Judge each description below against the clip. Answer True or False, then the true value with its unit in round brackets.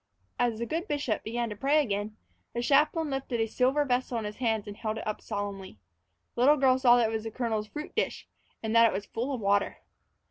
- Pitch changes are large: False (3.7 semitones)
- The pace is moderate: False (235 wpm)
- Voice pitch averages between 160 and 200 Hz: False (235 Hz)